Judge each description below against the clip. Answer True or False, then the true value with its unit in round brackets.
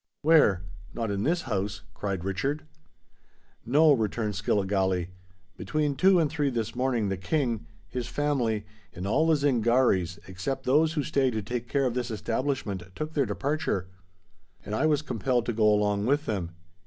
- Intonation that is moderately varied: False (5.9 semitones)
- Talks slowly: False (165 wpm)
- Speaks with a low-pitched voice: True (120 Hz)